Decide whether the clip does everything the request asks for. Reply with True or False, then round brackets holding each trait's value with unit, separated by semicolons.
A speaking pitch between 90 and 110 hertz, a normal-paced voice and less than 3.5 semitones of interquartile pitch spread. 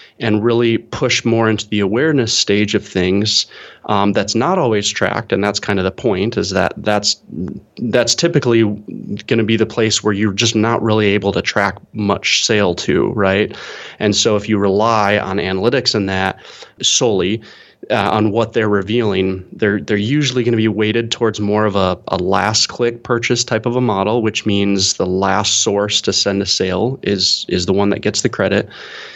True (105 Hz; 195 wpm; 2.5 semitones)